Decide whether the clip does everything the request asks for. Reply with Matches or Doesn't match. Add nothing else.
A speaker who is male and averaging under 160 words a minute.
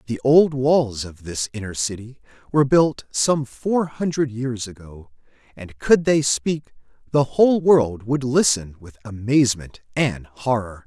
Matches